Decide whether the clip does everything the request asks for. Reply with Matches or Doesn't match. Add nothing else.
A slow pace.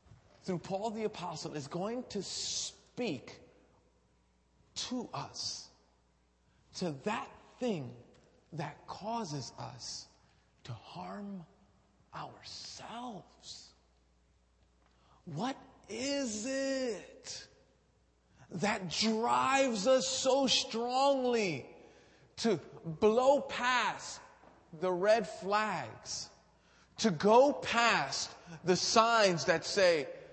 Matches